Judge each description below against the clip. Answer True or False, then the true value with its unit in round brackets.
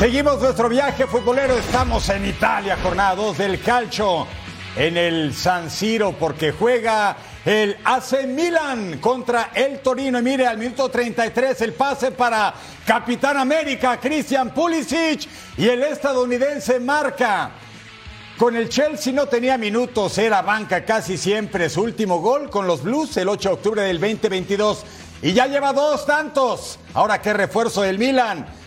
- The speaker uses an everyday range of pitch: True (5.0 semitones)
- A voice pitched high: True (230 Hz)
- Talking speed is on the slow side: False (150 wpm)